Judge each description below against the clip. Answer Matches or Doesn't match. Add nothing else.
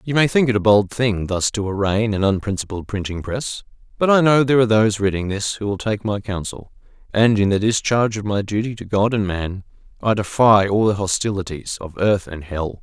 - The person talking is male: Matches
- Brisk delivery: Matches